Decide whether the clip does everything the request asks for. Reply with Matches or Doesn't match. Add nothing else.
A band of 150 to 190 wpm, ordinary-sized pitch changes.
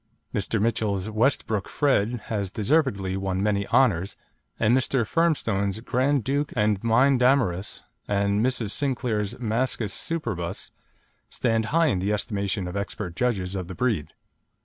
Doesn't match